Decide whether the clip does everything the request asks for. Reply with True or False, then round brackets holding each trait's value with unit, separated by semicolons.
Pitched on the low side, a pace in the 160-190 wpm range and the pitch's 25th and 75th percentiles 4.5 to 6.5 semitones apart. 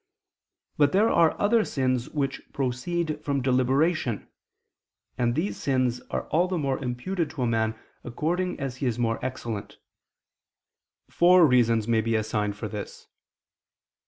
False (130 Hz; 135 wpm; 5.3 semitones)